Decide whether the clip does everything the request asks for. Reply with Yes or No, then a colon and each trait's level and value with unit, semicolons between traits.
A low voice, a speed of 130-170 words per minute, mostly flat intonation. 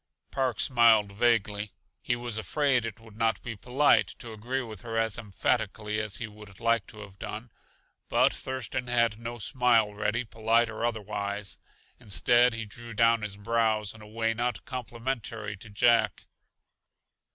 Yes: low, 115 Hz; average, 160 wpm; narrow, 2.1 semitones